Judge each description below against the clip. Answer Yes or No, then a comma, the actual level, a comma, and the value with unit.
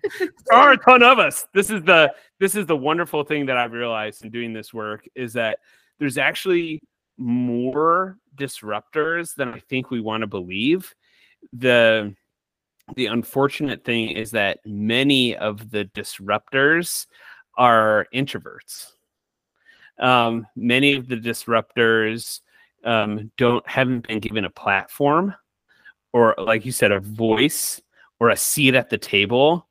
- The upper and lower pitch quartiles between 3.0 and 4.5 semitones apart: No, average, 4.9 semitones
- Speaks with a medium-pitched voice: No, low, 125 Hz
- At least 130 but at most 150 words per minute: Yes, average, 140 wpm